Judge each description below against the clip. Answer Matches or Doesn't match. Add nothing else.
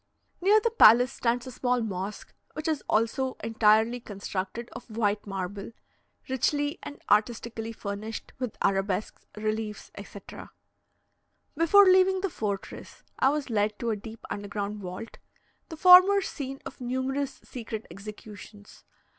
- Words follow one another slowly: Matches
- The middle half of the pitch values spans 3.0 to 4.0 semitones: Doesn't match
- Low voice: Doesn't match